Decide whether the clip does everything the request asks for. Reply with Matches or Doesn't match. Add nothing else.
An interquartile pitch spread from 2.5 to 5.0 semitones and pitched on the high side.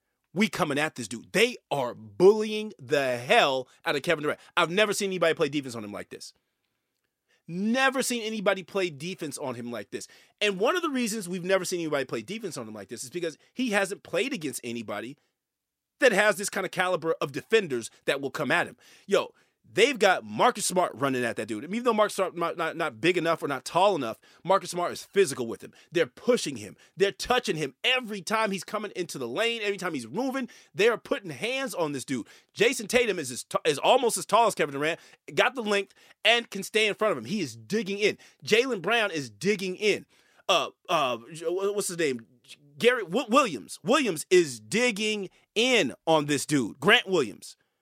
Doesn't match